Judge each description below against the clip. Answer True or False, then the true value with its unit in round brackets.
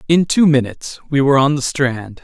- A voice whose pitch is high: False (140 Hz)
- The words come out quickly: True (215 wpm)